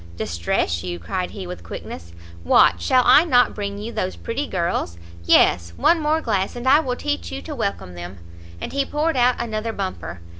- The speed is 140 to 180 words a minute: No, average, 190 wpm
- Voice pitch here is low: No, high, 190 Hz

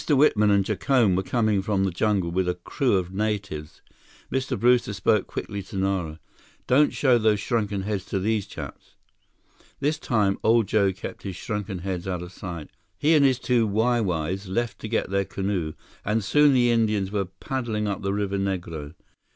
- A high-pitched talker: No, low, 100 Hz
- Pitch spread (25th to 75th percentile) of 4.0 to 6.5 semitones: No, average, 3.3 semitones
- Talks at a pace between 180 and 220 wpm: Yes, average, 185 wpm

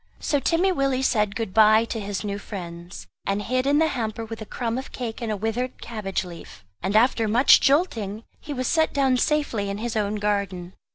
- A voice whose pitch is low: No, high, 225 Hz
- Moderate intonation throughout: Yes, average, 4.0 semitones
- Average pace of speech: No, fast, 210 wpm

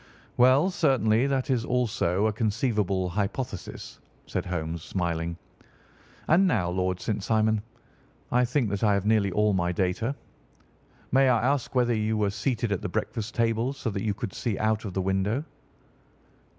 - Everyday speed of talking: Yes, average, 165 wpm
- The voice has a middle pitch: No, low, 110 Hz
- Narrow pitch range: No, average, 4.2 semitones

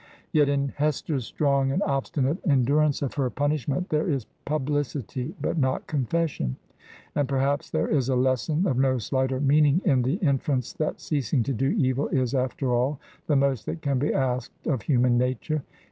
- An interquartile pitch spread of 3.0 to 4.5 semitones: No, narrow, 2.4 semitones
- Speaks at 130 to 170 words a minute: No, average, 185 wpm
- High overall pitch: No, low, 135 Hz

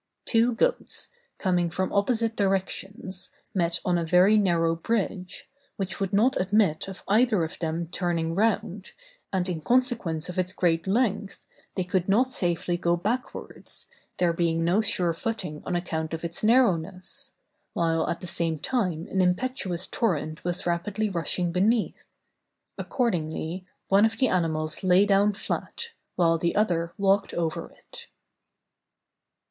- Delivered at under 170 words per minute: Yes, average, 145 wpm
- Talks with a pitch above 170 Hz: Yes, medium, 185 Hz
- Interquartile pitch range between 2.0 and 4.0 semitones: Yes, average, 3.7 semitones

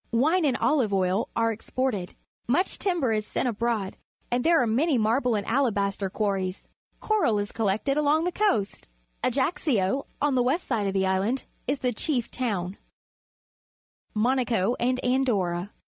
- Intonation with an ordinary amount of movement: Yes, average, 4.8 semitones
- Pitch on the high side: Yes, high, 235 Hz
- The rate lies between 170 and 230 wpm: No, average, 150 wpm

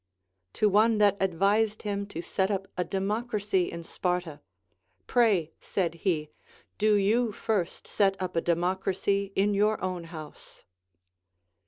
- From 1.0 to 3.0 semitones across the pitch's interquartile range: Yes, average, 2.7 semitones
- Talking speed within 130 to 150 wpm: Yes, average, 140 wpm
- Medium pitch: No, high, 195 Hz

